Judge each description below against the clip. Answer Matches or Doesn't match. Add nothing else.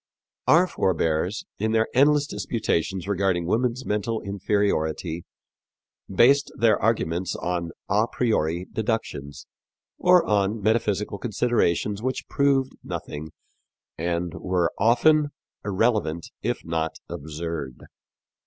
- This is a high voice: Doesn't match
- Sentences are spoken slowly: Matches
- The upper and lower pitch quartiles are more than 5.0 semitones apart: Matches